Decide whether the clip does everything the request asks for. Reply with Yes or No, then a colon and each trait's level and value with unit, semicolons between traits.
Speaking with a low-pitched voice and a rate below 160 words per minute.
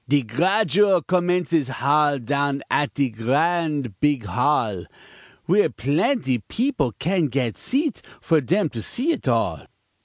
No: medium, 145 Hz; slow, 135 wpm